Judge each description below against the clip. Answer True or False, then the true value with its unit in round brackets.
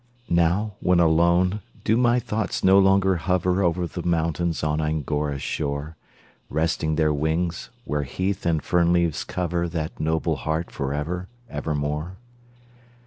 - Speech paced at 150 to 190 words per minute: False (140 wpm)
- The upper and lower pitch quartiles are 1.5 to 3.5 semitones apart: True (2.8 semitones)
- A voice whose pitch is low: True (85 Hz)